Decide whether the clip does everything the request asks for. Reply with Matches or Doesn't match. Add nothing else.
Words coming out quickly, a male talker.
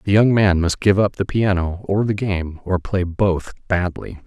Matches